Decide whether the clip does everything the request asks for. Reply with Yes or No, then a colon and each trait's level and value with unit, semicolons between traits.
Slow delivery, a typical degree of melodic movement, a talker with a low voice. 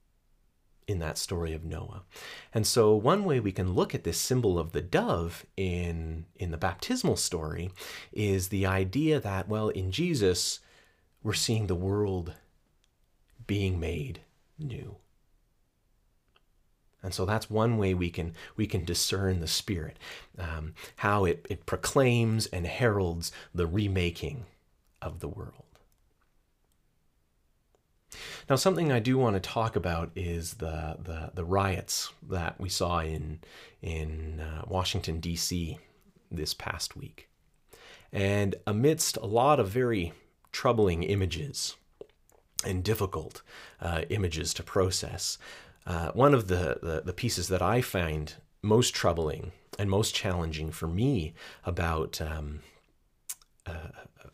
Yes: slow, 130 wpm; average, 4.2 semitones; very low, 95 Hz